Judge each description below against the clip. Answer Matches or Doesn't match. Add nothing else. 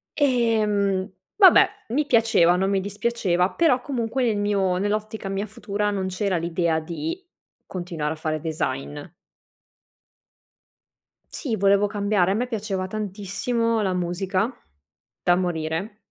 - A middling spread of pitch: Matches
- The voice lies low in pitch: Doesn't match